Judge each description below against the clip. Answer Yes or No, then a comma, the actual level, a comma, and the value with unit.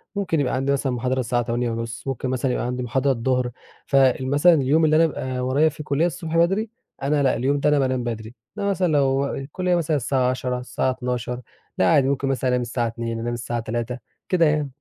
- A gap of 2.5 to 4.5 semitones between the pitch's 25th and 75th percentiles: Yes, average, 3.2 semitones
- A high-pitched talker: No, low, 130 Hz